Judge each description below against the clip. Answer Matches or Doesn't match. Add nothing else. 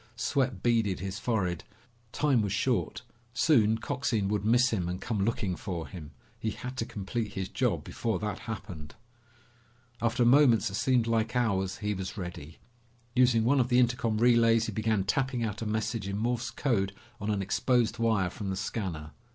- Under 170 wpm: Doesn't match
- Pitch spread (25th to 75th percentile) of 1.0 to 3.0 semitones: Doesn't match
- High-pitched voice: Doesn't match